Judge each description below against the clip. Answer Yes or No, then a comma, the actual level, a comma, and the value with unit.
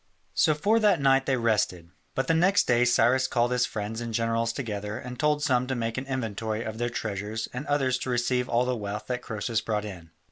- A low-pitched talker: Yes, low, 120 Hz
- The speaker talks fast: Yes, fast, 225 wpm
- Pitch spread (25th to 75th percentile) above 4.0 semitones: No, average, 3.0 semitones